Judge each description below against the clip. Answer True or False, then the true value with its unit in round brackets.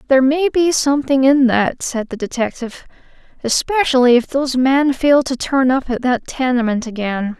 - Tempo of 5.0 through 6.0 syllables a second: True (5.1 syllables/s)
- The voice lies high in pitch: True (260 Hz)